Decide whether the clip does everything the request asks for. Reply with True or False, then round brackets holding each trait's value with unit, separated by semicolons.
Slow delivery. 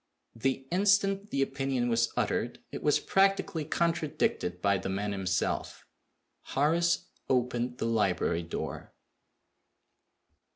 True (110 wpm)